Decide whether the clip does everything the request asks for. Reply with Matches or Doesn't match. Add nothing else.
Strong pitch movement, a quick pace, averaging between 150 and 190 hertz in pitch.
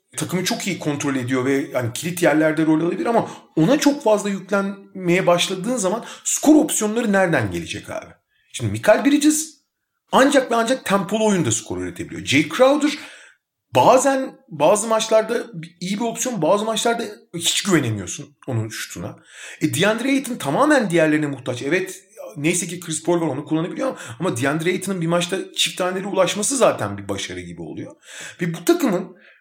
Matches